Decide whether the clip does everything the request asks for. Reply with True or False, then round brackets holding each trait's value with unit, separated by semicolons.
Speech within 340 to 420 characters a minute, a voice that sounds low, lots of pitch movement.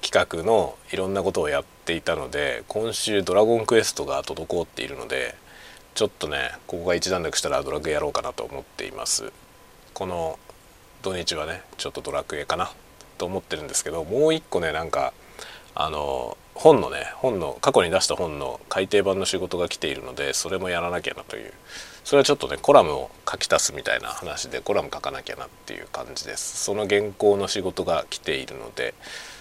False (390 characters per minute; 105 Hz; 2.3 semitones)